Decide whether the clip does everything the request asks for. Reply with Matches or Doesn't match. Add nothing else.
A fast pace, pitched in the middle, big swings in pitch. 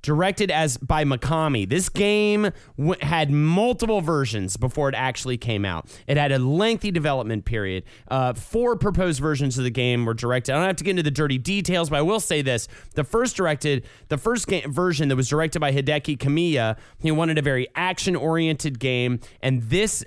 Doesn't match